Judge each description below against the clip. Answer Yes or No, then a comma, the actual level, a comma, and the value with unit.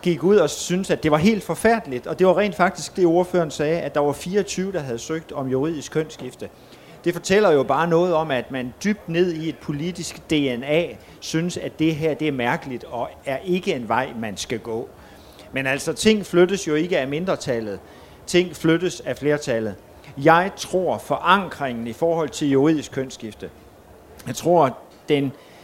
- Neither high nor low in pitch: Yes, medium, 160 Hz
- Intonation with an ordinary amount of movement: Yes, average, 4.6 semitones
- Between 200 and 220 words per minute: No, average, 185 wpm